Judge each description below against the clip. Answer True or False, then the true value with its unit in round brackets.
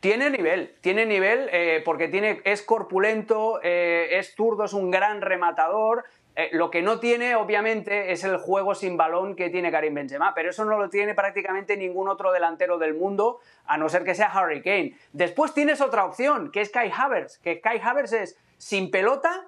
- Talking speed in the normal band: False (195 wpm)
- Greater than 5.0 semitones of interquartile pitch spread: False (3.5 semitones)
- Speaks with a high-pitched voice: True (195 Hz)